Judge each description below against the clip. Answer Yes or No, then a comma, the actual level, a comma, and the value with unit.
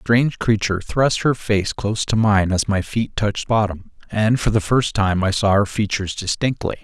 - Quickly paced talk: Yes, fast, 210 wpm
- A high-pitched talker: No, low, 105 Hz